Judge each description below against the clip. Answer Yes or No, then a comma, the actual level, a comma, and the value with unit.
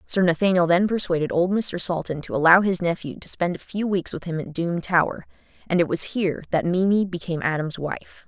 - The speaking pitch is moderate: Yes, medium, 175 Hz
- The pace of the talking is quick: Yes, fast, 220 wpm